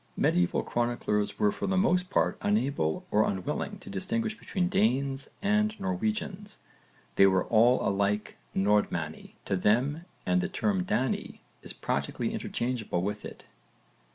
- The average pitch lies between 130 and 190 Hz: Yes, medium, 140 Hz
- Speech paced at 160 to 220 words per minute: No, slow, 135 wpm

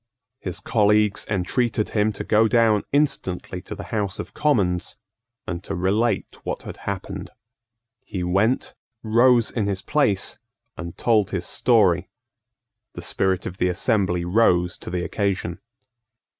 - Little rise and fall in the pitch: No, average, 3.6 semitones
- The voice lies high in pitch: No, low, 100 Hz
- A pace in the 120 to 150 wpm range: Yes, average, 140 wpm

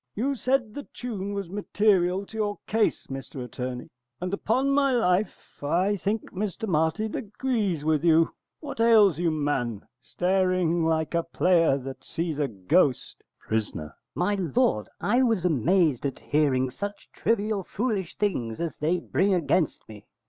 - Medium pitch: Yes, medium, 180 Hz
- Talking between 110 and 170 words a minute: Yes, average, 155 wpm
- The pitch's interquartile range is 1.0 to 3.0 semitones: No, wide, 5.6 semitones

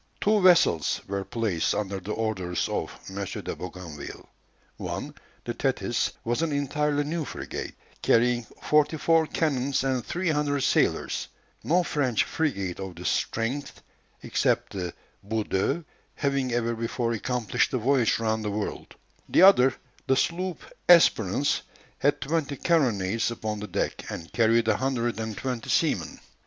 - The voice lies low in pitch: Yes, low, 120 Hz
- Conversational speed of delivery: Yes, average, 145 wpm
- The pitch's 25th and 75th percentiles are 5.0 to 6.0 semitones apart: Yes, wide, 5.4 semitones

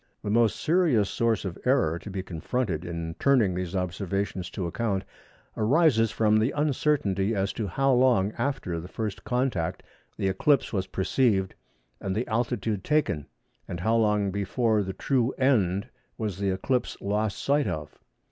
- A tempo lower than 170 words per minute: Yes, average, 155 wpm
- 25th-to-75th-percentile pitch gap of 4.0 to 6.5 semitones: Yes, average, 4.7 semitones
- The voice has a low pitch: Yes, low, 105 Hz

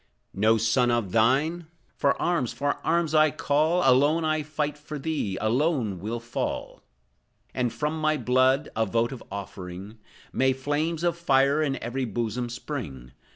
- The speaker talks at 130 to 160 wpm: Yes, average, 150 wpm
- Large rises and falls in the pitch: No, average, 5.0 semitones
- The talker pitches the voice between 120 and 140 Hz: Yes, low, 135 Hz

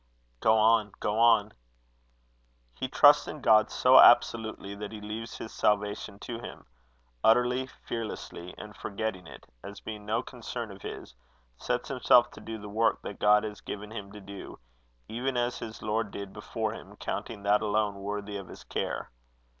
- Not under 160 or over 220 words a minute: Yes, average, 170 wpm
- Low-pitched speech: Yes, low, 110 Hz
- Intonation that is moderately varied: No, narrow, 1.9 semitones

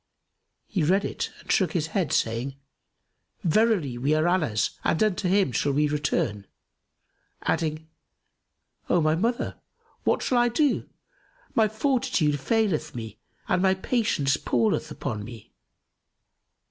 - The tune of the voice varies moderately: No, wide, 7.3 semitones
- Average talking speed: No, slow, 130 wpm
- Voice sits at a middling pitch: Yes, medium, 160 Hz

